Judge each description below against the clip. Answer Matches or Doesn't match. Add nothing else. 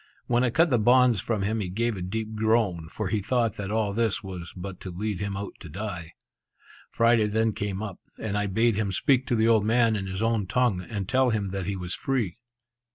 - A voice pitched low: Matches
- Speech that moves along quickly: Matches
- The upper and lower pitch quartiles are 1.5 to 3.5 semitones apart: Matches